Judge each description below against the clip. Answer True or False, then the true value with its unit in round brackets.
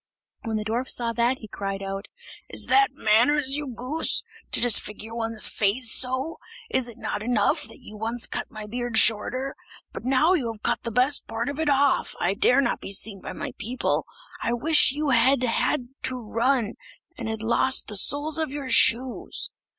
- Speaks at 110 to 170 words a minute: False (190 wpm)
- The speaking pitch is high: True (240 Hz)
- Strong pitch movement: False (3.4 semitones)